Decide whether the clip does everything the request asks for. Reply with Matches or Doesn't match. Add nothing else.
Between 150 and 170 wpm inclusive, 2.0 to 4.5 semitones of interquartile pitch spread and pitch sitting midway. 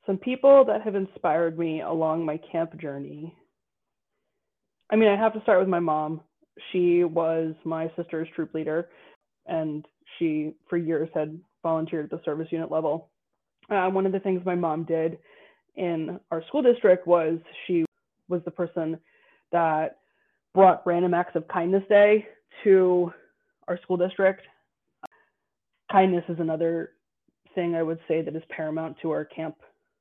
Matches